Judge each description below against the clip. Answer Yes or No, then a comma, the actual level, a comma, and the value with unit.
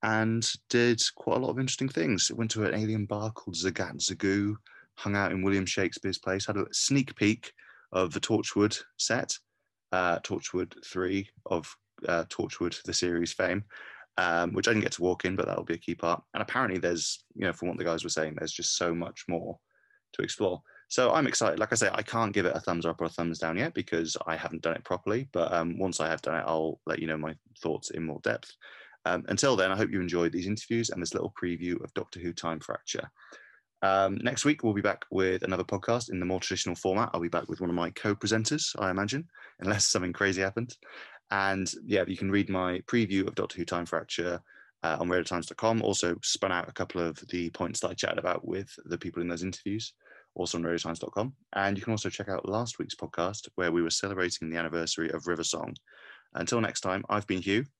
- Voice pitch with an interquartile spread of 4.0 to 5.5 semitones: No, average, 3.5 semitones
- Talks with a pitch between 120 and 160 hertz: No, very low, 95 Hz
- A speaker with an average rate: No, fast, 225 wpm